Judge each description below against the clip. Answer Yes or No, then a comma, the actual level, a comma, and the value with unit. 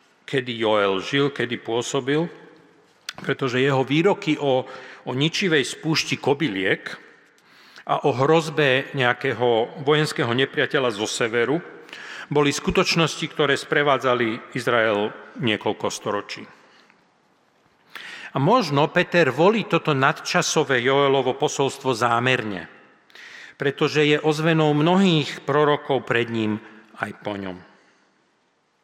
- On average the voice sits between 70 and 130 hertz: No, medium, 140 Hz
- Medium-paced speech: No, slow, 100 wpm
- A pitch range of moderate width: Yes, average, 3.4 semitones